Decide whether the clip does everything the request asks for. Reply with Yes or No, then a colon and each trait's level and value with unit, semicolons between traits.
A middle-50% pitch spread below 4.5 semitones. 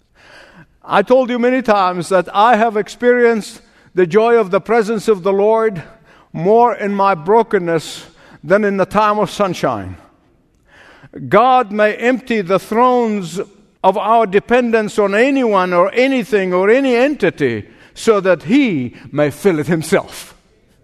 Yes: average, 3.7 semitones